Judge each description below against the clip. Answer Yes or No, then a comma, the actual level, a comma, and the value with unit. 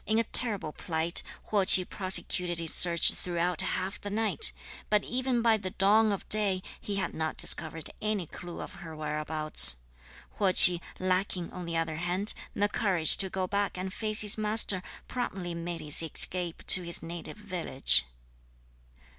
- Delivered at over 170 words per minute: No, average, 165 wpm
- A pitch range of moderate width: Yes, average, 3.5 semitones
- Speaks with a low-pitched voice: No, medium, 185 Hz